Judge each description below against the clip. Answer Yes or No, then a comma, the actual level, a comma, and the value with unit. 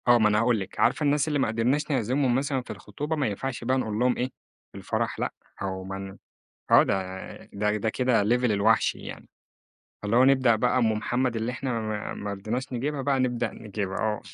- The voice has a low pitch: Yes, low, 120 Hz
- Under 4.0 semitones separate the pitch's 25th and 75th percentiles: Yes, average, 3.6 semitones